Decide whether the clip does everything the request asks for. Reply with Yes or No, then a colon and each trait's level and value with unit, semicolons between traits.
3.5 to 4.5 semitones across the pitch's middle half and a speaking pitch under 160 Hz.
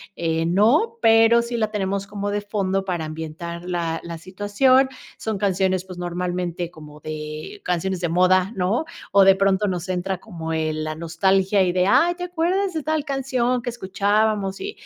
No: average, 4.2 semitones; high, 190 Hz